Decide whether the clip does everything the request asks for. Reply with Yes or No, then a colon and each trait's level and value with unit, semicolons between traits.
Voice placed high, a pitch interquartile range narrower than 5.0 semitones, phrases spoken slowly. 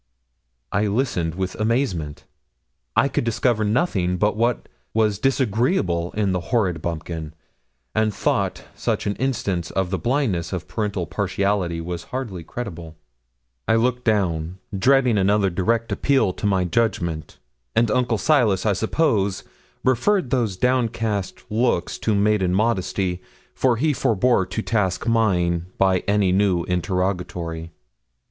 No: low, 100 Hz; average, 4.5 semitones; slow, 130 wpm